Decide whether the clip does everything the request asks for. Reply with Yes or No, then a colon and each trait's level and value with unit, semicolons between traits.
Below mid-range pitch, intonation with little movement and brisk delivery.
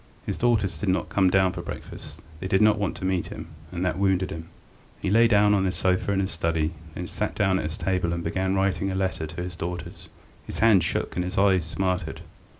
Yes: very low, 95 Hz; narrow, 1.7 semitones; fast, 235 wpm